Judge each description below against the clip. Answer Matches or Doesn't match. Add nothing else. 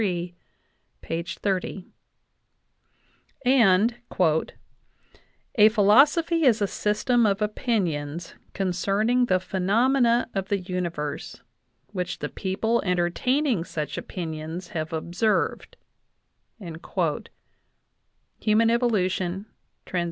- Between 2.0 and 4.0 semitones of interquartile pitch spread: Doesn't match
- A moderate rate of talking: Doesn't match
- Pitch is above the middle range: Matches